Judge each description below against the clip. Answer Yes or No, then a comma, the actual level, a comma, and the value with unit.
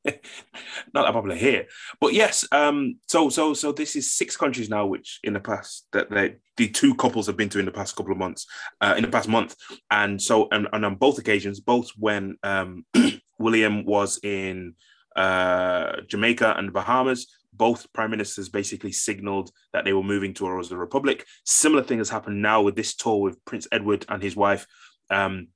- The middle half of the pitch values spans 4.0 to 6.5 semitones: Yes, average, 4.7 semitones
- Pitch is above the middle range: No, low, 105 Hz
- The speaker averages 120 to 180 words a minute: No, average, 195 wpm